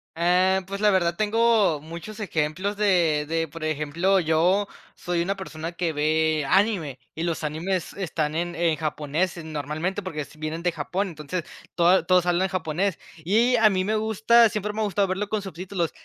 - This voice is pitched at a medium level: Yes, medium, 175 Hz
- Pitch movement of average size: Yes, average, 3.8 semitones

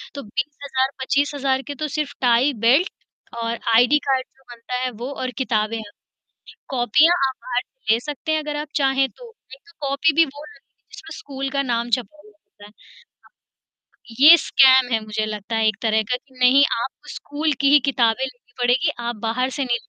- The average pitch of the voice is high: Yes, very high, 260 Hz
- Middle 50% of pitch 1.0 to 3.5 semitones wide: Yes, average, 3.2 semitones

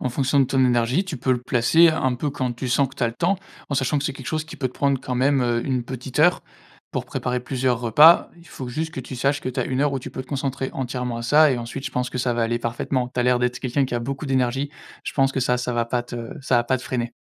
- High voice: No, low, 130 Hz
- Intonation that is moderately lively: No, narrow, 2.1 semitones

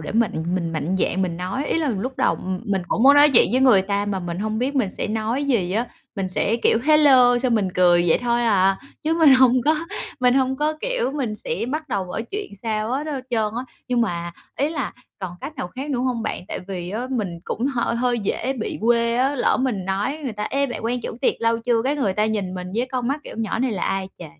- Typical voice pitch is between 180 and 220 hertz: No, high, 235 Hz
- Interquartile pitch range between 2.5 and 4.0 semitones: No, average, 5.2 semitones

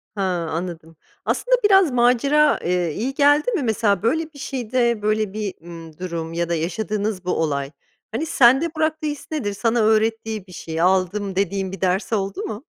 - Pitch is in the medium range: No, high, 215 Hz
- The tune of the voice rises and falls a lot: Yes, wide, 6.1 semitones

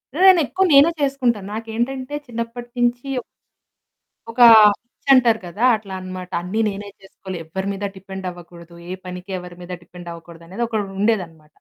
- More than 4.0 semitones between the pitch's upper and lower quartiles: Yes, average, 5.0 semitones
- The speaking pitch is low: No, high, 200 Hz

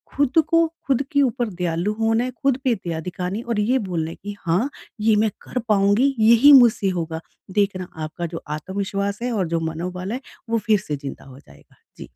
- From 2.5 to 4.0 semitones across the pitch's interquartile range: No, average, 5.0 semitones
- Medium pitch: No, high, 205 Hz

